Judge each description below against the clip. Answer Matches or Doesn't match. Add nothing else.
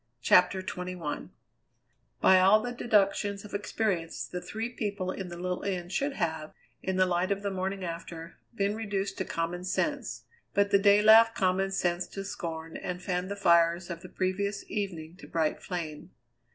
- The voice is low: Doesn't match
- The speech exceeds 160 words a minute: Matches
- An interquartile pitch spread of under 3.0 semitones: Matches